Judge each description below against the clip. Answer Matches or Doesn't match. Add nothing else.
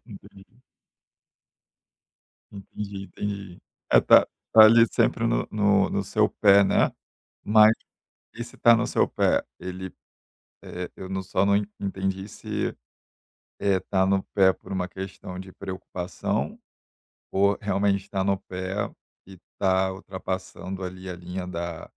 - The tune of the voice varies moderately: Doesn't match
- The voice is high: Doesn't match